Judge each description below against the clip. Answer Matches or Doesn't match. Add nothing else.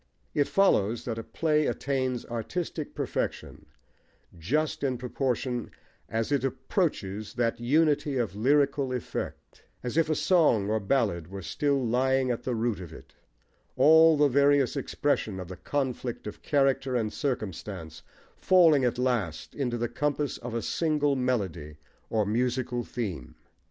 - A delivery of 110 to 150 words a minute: Matches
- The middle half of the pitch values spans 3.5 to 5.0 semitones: Matches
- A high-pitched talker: Doesn't match